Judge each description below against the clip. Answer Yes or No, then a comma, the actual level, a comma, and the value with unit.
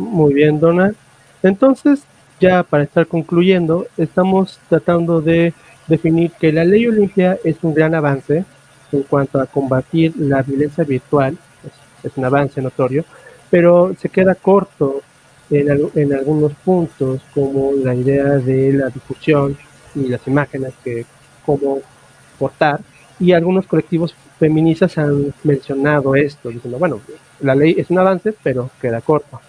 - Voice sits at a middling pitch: Yes, medium, 145 Hz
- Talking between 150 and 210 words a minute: No, average, 140 wpm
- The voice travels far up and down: No, average, 3.7 semitones